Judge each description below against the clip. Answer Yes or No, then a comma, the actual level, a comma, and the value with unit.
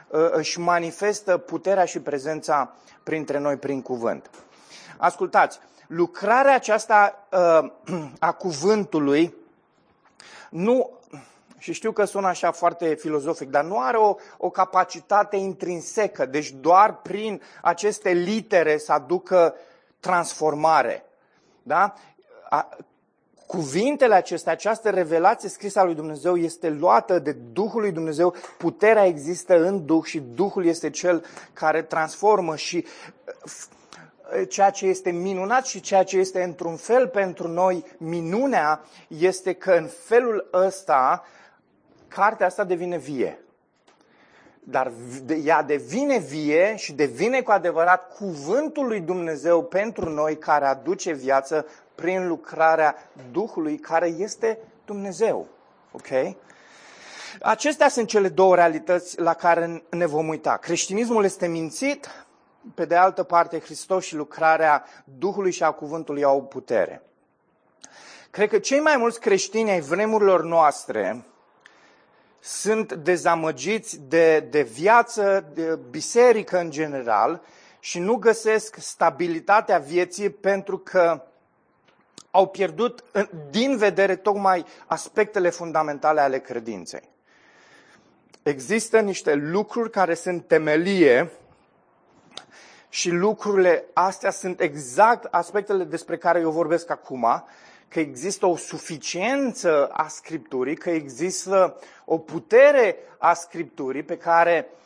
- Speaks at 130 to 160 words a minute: No, slow, 115 wpm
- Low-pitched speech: No, medium, 175 Hz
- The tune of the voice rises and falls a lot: No, average, 4.0 semitones